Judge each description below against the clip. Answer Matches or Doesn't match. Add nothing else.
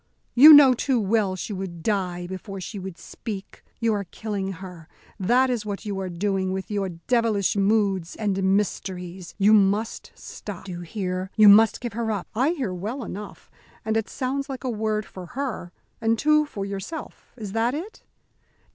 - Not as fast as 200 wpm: Matches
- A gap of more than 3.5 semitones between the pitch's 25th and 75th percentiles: Doesn't match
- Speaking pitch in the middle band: Doesn't match